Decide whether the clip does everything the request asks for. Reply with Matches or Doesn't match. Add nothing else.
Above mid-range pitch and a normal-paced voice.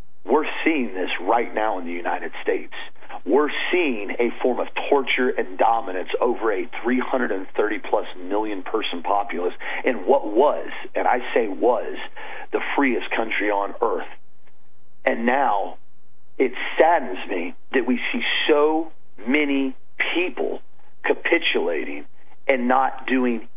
Doesn't match